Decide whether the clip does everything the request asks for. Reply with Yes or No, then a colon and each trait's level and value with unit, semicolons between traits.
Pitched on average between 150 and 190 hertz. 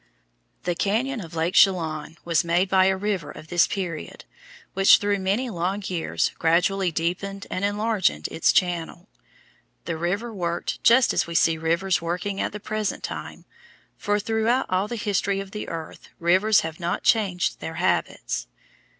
Yes: medium, 185 Hz